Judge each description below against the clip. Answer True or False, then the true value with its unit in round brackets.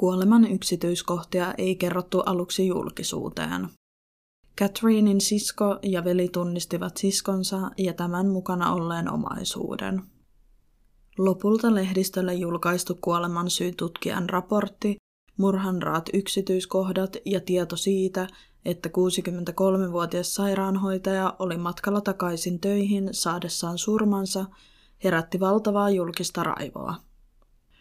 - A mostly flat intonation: True (1.8 semitones)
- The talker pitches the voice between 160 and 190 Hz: True (185 Hz)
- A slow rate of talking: True (90 wpm)